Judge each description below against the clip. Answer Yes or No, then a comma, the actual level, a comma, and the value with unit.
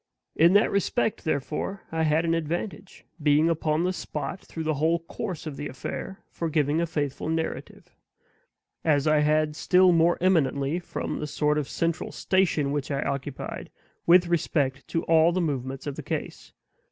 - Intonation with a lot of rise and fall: No, narrow, 2.6 semitones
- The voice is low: No, medium, 160 Hz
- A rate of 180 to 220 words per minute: No, average, 170 wpm